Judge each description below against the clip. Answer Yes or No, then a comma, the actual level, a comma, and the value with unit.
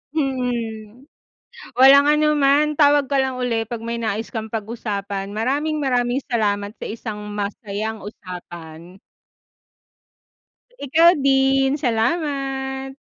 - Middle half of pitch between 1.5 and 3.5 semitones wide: No, average, 4.1 semitones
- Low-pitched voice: No, high, 245 Hz